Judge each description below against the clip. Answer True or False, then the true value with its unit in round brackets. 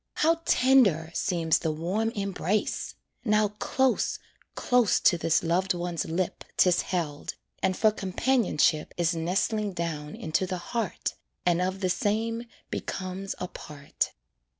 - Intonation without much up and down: False (4.1 semitones)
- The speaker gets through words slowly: True (130 wpm)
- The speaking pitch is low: False (185 Hz)